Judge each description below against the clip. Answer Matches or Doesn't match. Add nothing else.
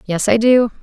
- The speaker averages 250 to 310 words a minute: Doesn't match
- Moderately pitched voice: Doesn't match